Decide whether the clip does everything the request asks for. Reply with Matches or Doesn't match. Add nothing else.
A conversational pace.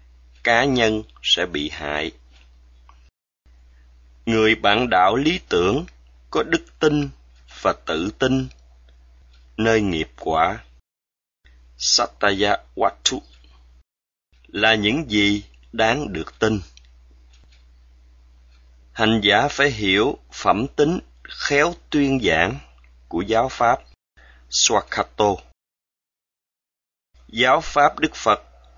Doesn't match